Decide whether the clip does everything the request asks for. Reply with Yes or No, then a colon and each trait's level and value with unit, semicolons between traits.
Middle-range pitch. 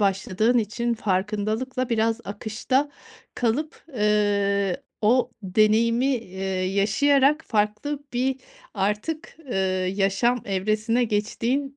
No: high, 220 Hz